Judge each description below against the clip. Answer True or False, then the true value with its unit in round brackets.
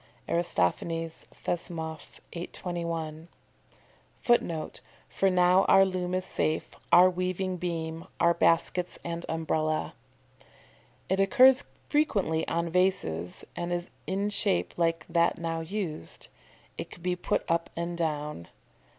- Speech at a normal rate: False (115 wpm)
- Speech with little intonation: True (2.1 semitones)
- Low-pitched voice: False (170 Hz)